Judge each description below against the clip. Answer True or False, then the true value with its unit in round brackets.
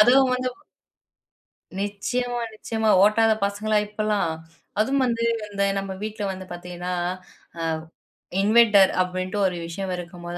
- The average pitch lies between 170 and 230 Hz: True (205 Hz)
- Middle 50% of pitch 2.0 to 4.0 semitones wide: True (3.5 semitones)